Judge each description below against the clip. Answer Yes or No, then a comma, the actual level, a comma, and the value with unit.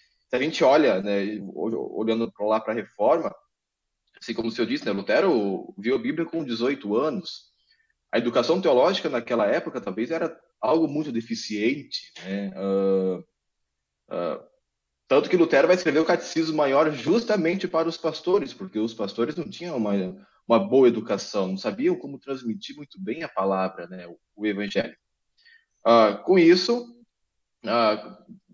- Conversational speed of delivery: Yes, average, 155 wpm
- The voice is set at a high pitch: No, low, 135 Hz